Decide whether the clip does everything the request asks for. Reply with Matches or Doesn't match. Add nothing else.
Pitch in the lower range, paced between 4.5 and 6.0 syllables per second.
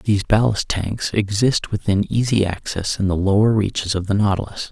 Matches